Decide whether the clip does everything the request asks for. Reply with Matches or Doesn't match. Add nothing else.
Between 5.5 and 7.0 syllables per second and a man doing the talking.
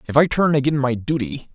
Matches